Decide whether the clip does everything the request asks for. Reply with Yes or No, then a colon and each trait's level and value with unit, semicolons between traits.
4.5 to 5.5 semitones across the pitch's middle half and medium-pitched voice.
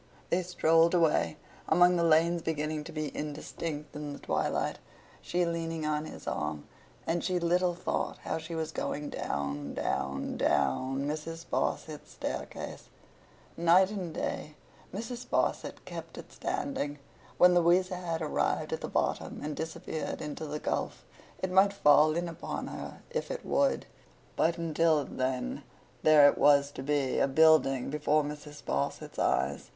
No: average, 2.7 semitones; medium, 160 Hz